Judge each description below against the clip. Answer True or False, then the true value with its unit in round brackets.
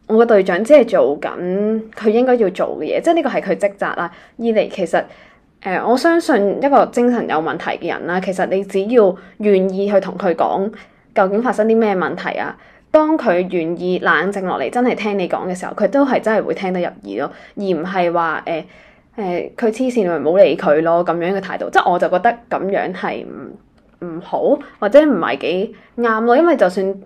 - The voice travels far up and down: False (4.5 semitones)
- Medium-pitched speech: False (200 Hz)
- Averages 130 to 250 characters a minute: False (295 characters per minute)